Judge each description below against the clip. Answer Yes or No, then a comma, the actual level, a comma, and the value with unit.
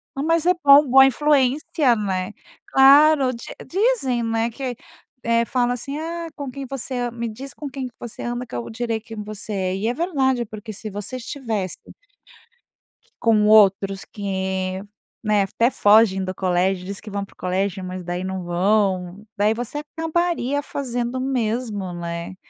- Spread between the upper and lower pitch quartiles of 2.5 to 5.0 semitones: No, wide, 5.4 semitones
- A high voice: Yes, high, 230 Hz